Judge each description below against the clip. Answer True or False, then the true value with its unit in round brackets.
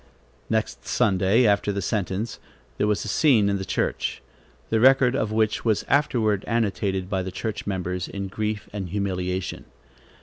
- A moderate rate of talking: True (160 wpm)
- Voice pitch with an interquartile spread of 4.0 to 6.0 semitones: False (2.6 semitones)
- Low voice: True (100 Hz)